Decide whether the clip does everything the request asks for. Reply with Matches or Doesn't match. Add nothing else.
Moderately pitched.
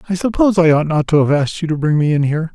Matches